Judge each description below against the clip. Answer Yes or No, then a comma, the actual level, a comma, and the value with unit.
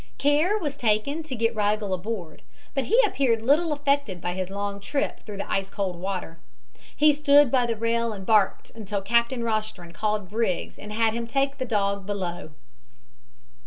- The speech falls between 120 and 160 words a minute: No, average, 175 wpm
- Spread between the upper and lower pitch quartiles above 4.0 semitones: Yes, wide, 5.4 semitones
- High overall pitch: Yes, high, 220 Hz